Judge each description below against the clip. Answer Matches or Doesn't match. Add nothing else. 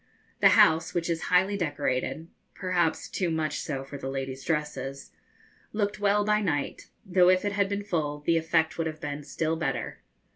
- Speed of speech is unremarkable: Matches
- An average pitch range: Matches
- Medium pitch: Matches